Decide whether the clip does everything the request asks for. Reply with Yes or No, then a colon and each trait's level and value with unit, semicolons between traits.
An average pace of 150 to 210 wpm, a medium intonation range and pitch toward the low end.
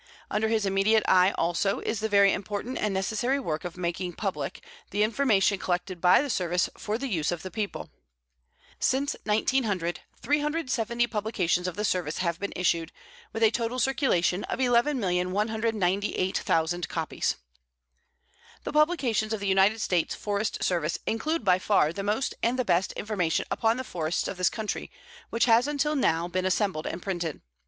No: average, 165 wpm; average, 4.3 semitones; high, 205 Hz